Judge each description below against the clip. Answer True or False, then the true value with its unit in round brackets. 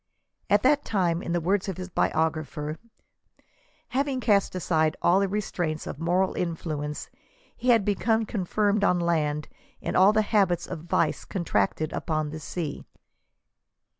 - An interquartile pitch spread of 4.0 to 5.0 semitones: True (4.5 semitones)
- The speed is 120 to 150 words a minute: False (160 wpm)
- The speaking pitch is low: False (175 Hz)